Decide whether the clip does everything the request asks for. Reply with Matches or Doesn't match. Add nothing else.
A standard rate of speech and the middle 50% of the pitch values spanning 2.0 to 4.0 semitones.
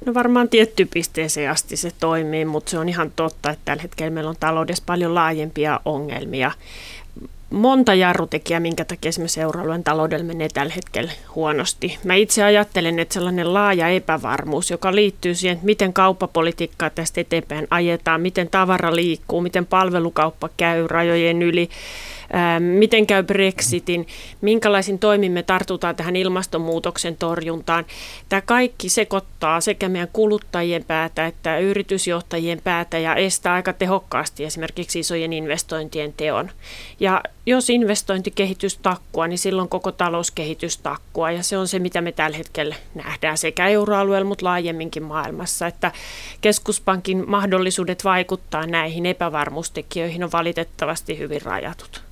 Matches